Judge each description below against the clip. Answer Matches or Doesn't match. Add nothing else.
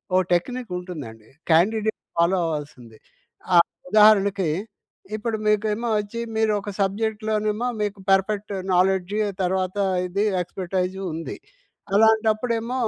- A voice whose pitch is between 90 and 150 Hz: Doesn't match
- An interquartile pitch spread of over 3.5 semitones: Doesn't match